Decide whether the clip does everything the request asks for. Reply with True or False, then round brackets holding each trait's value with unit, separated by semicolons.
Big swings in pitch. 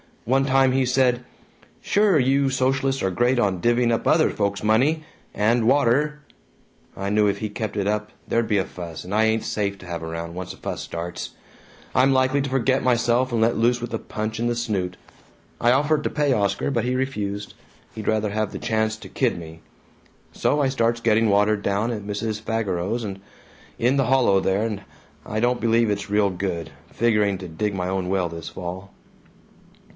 False (4.0 semitones)